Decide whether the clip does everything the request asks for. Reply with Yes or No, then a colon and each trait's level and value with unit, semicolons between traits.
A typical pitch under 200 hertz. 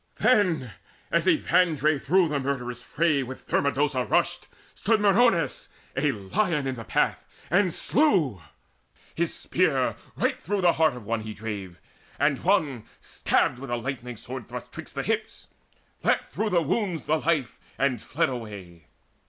Yes: medium, 140 Hz